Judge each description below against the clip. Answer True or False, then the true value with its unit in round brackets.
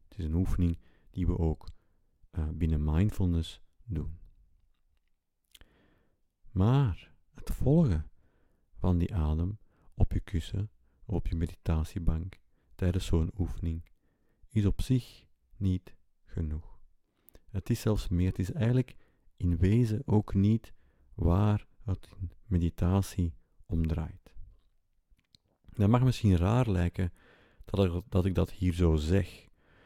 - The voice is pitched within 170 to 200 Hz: False (90 Hz)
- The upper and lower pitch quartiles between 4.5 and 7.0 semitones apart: False (3.2 semitones)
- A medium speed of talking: False (115 wpm)